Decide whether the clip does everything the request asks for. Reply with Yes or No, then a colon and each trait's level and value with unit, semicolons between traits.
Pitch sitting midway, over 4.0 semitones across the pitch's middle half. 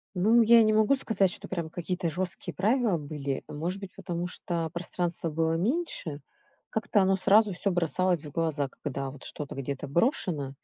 Yes: medium, 175 Hz; average, 4.5 semitones